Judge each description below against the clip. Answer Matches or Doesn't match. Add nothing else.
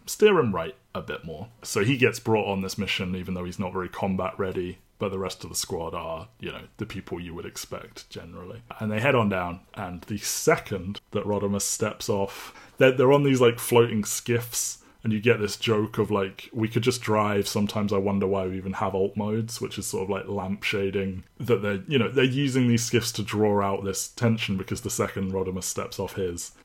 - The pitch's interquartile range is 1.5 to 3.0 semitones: Matches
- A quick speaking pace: Matches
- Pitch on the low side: Matches